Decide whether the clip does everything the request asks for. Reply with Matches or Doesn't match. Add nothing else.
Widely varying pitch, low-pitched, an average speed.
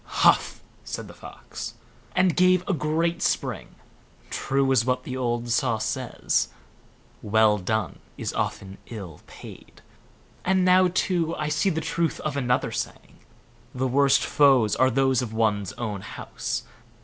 Matches